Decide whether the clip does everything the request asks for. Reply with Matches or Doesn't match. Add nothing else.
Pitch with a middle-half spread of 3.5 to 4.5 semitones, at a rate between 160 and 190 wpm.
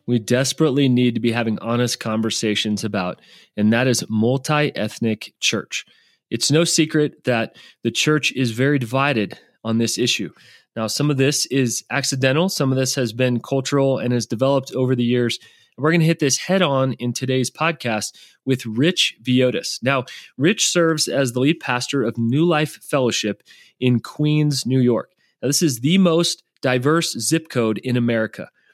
Matches